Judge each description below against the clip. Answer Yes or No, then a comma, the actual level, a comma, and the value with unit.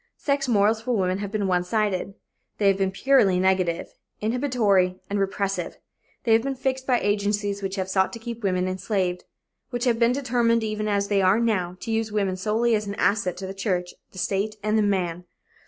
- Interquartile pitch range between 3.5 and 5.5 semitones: No, average, 3.1 semitones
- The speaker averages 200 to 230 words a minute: Yes, fast, 205 wpm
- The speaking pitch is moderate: No, high, 205 Hz